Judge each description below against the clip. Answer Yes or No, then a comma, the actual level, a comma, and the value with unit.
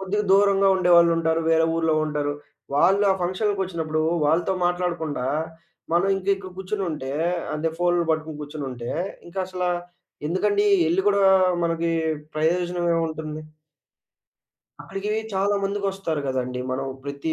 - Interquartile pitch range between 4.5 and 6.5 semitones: No, average, 3.6 semitones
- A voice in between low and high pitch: Yes, medium, 170 Hz